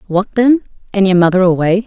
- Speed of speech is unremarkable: Yes, average, 195 wpm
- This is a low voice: No, high, 195 Hz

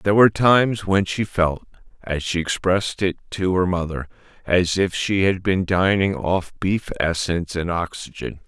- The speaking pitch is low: Yes, very low, 90 Hz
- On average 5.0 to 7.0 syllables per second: No, 4.7 syllables/s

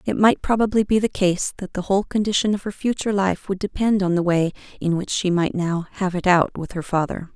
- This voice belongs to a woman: Yes, female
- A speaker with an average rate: No, fast, 245 wpm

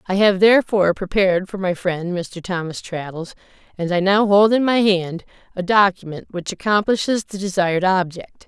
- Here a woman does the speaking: Yes, female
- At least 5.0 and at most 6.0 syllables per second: Yes, 5.2 syllables/s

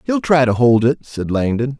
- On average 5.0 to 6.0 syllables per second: No, 4.8 syllables/s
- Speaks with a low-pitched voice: Yes, low, 130 Hz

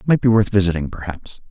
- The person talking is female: No, male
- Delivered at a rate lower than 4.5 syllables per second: No, 6.2 syllables/s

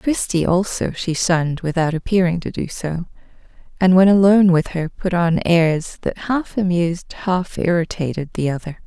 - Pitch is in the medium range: Yes, medium, 175 Hz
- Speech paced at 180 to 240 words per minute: No, average, 160 wpm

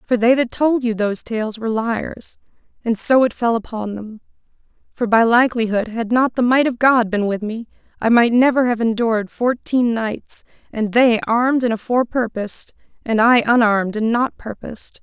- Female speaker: Yes, female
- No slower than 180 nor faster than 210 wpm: Yes, average, 185 wpm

